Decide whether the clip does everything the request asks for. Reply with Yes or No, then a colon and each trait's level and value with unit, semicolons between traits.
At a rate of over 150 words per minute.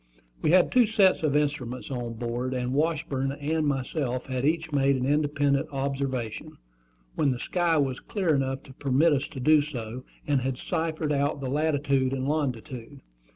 Yes: average, 170 wpm